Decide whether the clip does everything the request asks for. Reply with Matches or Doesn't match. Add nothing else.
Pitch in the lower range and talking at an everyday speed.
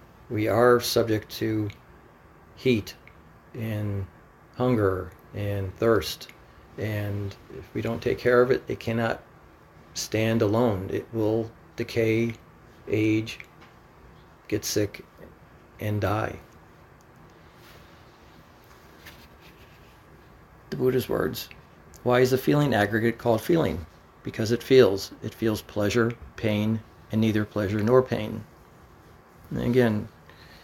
Doesn't match